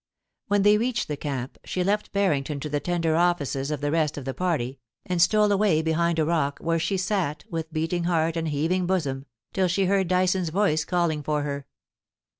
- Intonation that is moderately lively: Yes, average, 3.6 semitones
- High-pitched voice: No, medium, 165 Hz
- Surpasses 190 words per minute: Yes, average, 200 wpm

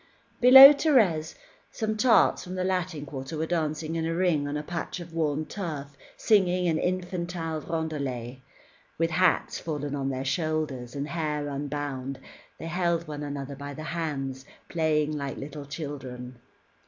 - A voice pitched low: No, medium, 155 Hz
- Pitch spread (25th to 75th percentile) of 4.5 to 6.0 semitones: No, average, 3.3 semitones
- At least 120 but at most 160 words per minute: Yes, average, 155 wpm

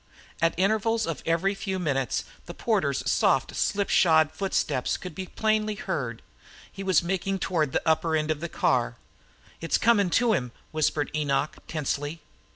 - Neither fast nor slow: Yes, average, 155 wpm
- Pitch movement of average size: Yes, average, 4.2 semitones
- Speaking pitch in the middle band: Yes, medium, 170 Hz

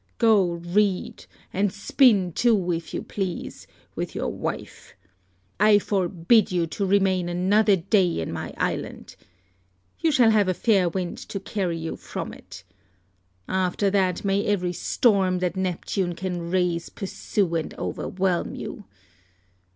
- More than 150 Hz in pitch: Yes, medium, 185 Hz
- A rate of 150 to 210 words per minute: No, slow, 135 wpm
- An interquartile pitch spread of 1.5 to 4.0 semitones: Yes, narrow, 2.5 semitones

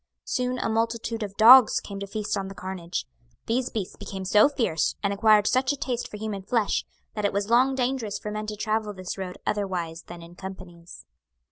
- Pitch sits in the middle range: No, high, 210 Hz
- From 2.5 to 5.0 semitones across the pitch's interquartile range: Yes, average, 3.2 semitones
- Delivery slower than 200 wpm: No, fast, 205 wpm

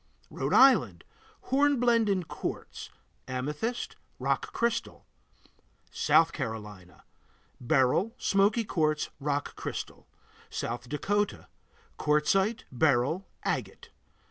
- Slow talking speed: Yes, slow, 85 wpm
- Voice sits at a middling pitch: Yes, medium, 160 Hz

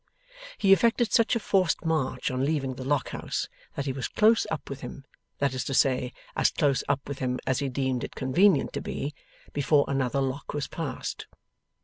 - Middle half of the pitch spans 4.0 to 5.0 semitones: No, average, 3.4 semitones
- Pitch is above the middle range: No, medium, 140 Hz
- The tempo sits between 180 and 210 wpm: Yes, average, 200 wpm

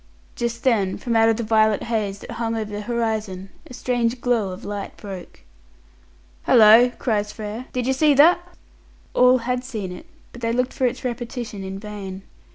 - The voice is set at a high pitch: Yes, high, 230 Hz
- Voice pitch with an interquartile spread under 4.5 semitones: Yes, average, 3.0 semitones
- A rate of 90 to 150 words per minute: No, average, 180 wpm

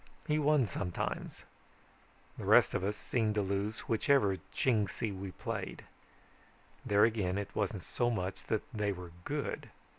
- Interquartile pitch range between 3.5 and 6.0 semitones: No, average, 3.0 semitones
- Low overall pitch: Yes, low, 105 Hz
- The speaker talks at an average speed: Yes, average, 145 wpm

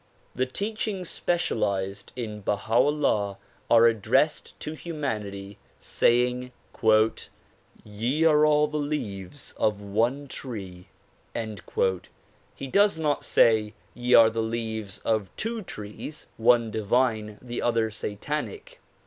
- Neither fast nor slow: No, slow, 115 wpm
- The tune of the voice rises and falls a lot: Yes, wide, 5.8 semitones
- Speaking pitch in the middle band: No, low, 115 Hz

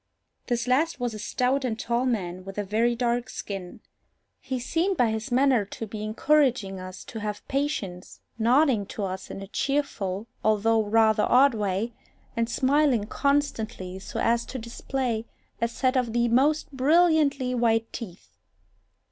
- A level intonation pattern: No, average, 3.8 semitones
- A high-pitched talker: Yes, high, 235 Hz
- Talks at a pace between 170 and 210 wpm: No, average, 155 wpm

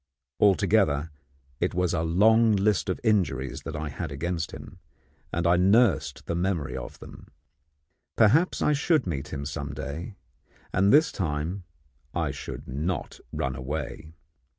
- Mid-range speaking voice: No, very low, 85 Hz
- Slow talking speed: No, average, 145 wpm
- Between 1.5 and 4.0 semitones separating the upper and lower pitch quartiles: No, wide, 5.5 semitones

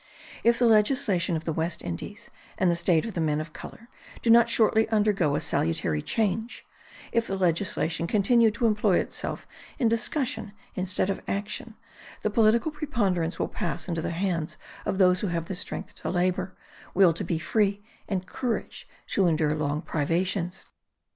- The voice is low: No, high, 190 Hz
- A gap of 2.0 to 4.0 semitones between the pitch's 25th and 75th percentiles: No, average, 4.7 semitones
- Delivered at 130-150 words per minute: No, average, 165 wpm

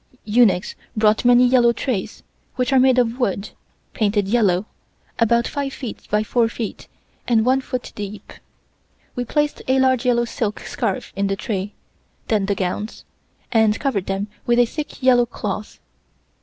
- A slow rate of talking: No, average, 155 wpm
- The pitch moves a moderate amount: Yes, average, 3.3 semitones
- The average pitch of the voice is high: Yes, high, 230 Hz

